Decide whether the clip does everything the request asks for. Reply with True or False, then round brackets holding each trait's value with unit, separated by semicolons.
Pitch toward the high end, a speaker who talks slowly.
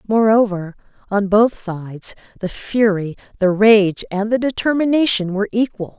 True (210 Hz; 130 wpm)